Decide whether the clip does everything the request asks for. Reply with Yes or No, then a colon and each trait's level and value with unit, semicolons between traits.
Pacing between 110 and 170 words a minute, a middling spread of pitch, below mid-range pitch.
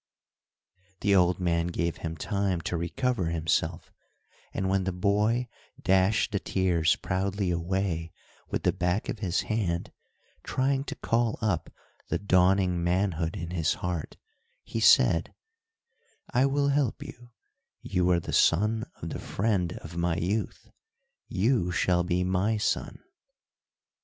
Yes: slow, 135 wpm; average, 3.4 semitones; very low, 95 Hz